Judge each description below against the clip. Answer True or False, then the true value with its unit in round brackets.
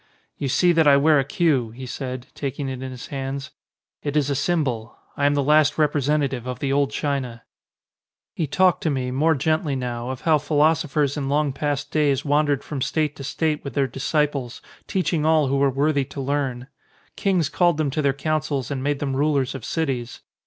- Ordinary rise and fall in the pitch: False (2.3 semitones)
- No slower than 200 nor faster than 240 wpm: True (205 wpm)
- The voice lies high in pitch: False (140 Hz)